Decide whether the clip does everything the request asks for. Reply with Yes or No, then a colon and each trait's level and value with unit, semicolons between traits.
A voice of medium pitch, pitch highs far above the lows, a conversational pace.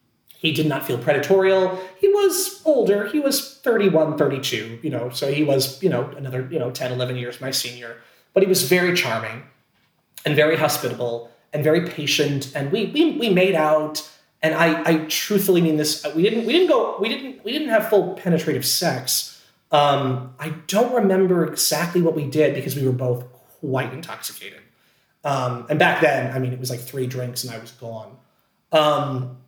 Yes: medium, 155 Hz; wide, 6.6 semitones; average, 190 wpm